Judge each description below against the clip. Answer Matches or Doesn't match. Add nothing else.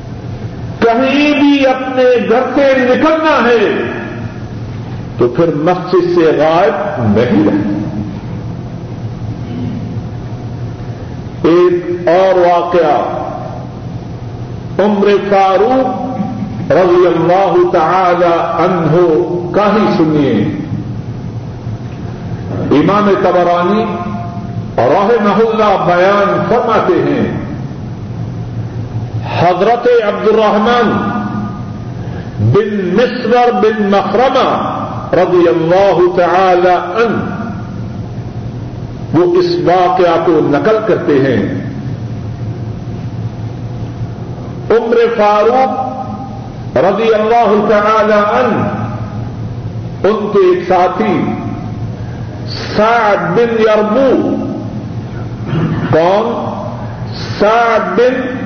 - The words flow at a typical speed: Doesn't match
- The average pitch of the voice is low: Doesn't match